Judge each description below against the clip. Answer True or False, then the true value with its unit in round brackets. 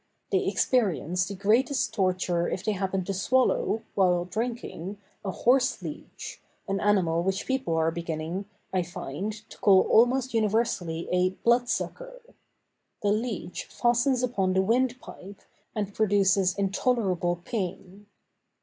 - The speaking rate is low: True (130 wpm)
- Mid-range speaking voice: False (195 Hz)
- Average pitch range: True (4.6 semitones)